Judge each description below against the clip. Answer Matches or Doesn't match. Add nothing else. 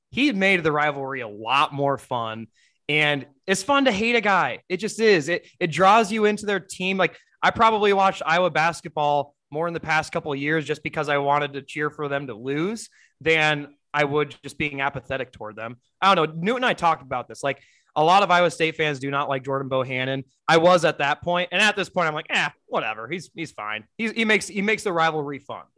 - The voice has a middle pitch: Matches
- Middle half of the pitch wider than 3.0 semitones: Matches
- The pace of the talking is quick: Matches